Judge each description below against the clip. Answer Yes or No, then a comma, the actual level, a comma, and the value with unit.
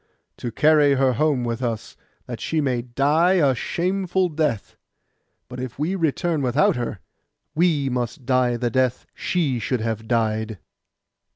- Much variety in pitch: No, average, 4.5 semitones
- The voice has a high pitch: No, low, 130 Hz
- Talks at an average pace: Yes, average, 150 wpm